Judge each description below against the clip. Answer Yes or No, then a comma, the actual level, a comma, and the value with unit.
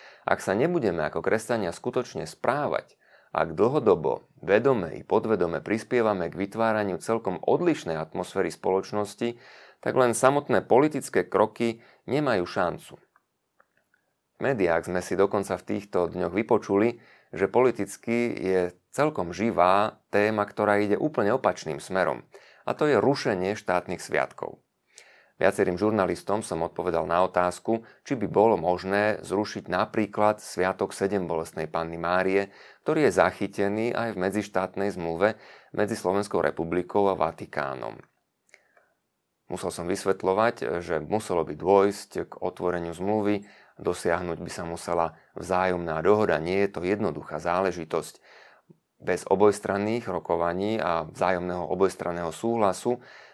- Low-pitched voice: Yes, very low, 95 Hz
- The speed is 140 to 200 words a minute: No, average, 125 wpm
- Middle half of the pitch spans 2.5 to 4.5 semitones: Yes, average, 2.9 semitones